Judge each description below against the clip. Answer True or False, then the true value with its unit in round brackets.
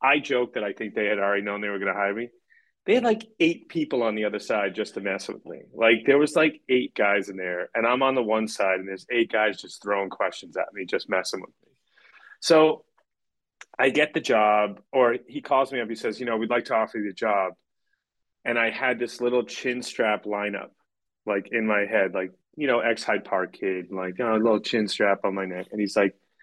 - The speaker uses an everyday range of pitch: True (3.9 semitones)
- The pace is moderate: False (250 wpm)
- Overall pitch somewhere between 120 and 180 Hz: False (110 Hz)